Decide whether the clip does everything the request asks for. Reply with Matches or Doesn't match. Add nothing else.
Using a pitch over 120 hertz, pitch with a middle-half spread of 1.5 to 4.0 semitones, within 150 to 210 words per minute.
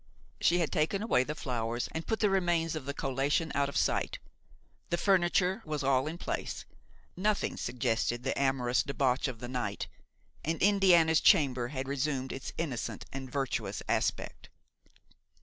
Doesn't match